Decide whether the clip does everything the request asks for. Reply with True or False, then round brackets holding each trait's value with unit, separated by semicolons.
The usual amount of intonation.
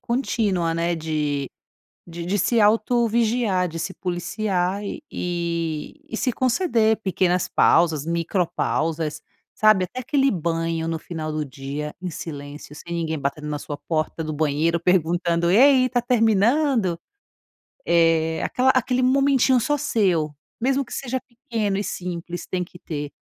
False (6.1 semitones)